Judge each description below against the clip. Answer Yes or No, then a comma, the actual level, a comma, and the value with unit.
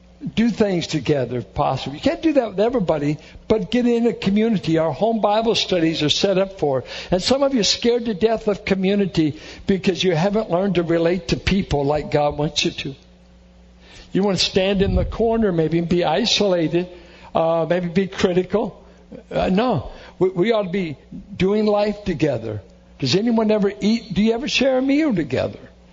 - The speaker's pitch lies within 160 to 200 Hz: Yes, high, 190 Hz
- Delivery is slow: No, average, 190 wpm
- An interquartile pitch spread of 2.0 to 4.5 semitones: No, average, 5.1 semitones